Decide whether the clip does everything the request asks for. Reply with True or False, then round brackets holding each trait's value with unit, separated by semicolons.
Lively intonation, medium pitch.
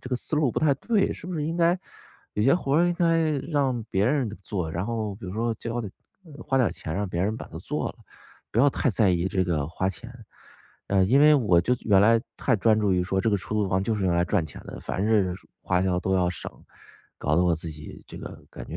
False (6.5 semitones; 105 Hz)